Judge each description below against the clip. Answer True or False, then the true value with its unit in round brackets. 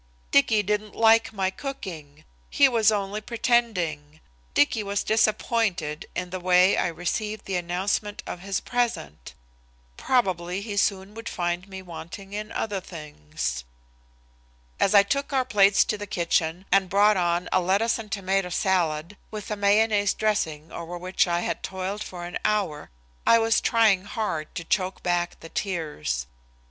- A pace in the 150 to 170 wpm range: True (155 wpm)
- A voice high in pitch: True (195 Hz)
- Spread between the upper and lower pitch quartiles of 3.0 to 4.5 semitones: True (3.5 semitones)